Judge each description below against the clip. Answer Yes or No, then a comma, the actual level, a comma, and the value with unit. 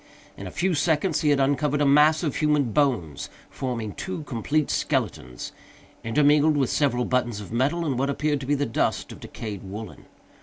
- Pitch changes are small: No, average, 4.2 semitones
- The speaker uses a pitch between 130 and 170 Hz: Yes, medium, 140 Hz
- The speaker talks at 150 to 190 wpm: Yes, average, 185 wpm